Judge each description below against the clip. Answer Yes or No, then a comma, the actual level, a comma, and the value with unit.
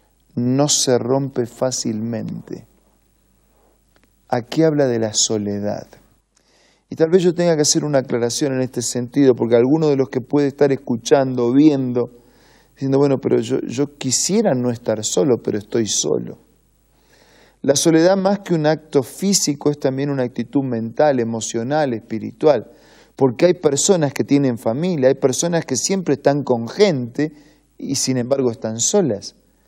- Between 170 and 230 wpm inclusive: No, average, 150 wpm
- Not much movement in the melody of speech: No, average, 3.7 semitones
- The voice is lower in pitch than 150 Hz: Yes, low, 135 Hz